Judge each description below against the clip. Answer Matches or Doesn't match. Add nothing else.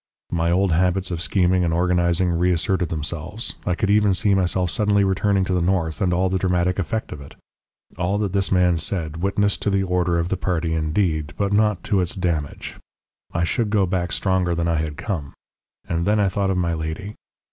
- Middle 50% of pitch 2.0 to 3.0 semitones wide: Matches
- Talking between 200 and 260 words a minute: Matches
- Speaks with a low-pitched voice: Matches